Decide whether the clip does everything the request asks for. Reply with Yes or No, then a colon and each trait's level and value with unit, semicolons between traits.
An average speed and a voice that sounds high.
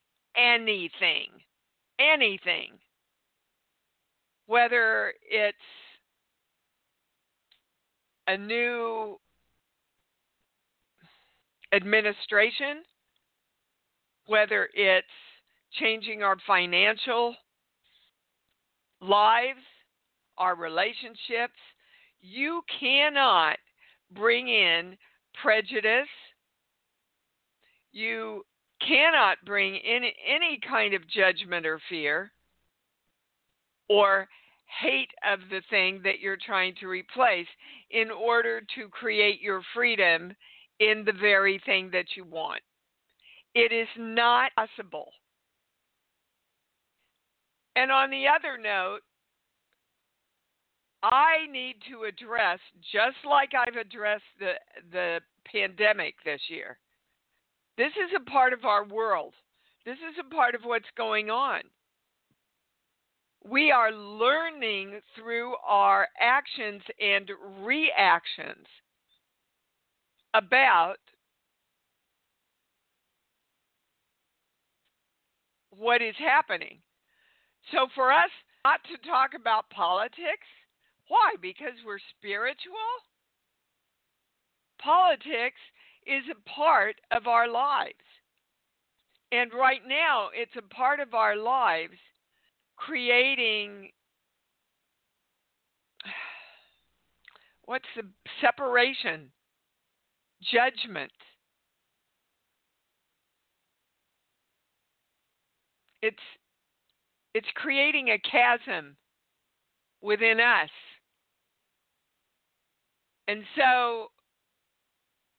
No: slow, 75 wpm; high, 225 Hz